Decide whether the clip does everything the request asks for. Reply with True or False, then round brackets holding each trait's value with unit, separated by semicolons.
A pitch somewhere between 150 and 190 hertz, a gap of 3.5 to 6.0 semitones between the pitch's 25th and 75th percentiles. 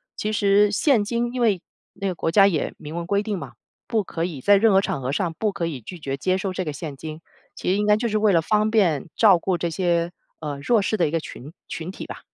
True (185 Hz; 4.2 semitones)